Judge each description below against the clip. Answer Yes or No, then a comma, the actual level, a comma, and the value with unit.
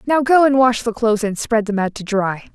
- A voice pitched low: No, high, 230 Hz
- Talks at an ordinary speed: No, fast, 280 wpm